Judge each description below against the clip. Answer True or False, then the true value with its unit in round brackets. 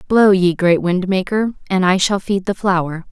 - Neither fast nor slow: False (210 wpm)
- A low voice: False (190 Hz)